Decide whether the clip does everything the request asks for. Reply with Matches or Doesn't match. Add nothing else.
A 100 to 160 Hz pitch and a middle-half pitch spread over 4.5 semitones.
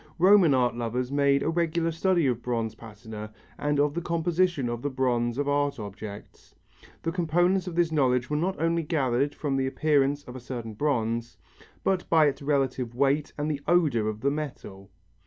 Matches